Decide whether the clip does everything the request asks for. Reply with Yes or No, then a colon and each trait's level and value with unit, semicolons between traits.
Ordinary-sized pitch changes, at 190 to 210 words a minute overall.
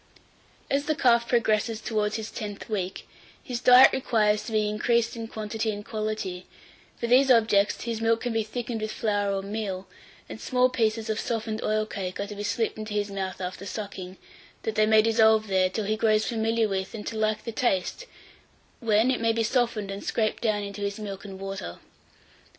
No: narrow, 1.9 semitones; average, 200 wpm